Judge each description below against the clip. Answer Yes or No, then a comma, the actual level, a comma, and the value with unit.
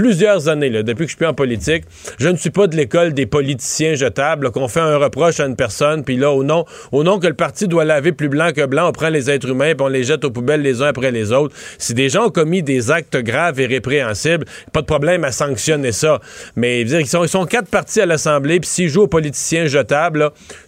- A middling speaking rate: No, fast, 265 wpm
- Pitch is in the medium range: Yes, medium, 150 Hz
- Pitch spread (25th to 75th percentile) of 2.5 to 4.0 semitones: Yes, average, 3.6 semitones